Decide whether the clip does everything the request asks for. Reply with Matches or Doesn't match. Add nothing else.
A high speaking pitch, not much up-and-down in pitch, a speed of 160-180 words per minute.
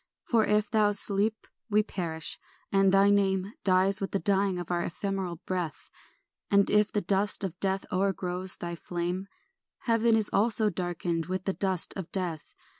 Matches